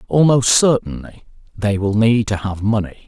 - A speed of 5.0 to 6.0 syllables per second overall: No, 4.8 syllables/s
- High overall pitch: No, low, 105 Hz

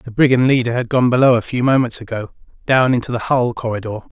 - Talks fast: Yes, fast, 215 wpm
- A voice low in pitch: Yes, low, 120 Hz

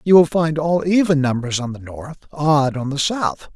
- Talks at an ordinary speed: No, fast, 220 wpm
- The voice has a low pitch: No, medium, 150 Hz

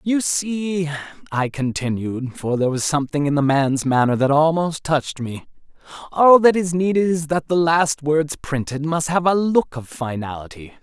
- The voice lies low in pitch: No, medium, 150 Hz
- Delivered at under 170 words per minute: No, average, 175 wpm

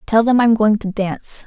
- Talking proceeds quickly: Yes, fast, 245 wpm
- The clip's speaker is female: Yes, female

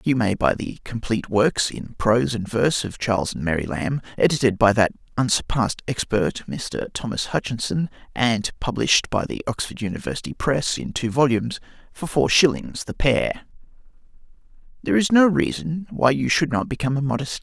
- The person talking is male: Yes, male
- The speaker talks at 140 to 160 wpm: No, average, 180 wpm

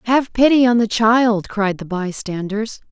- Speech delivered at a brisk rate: No, average, 165 wpm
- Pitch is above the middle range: Yes, high, 220 Hz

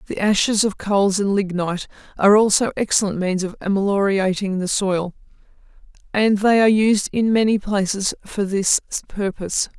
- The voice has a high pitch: Yes, high, 200 Hz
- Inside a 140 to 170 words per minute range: Yes, average, 145 wpm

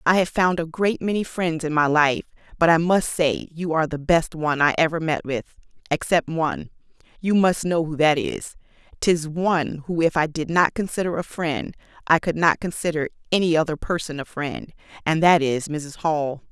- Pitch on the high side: No, medium, 160 Hz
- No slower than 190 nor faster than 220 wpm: Yes, average, 200 wpm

